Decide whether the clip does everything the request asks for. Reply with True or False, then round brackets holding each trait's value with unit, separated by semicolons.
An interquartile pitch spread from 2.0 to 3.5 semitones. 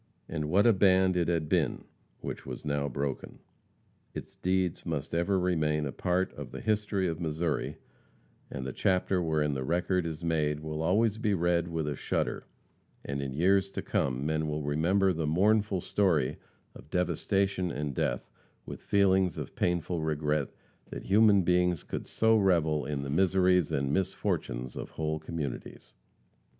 False (3.9 semitones)